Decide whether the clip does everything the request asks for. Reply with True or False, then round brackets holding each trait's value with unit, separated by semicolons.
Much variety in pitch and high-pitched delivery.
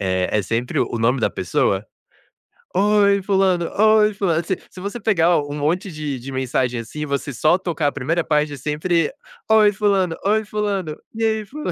False (5.9 semitones; 170 Hz)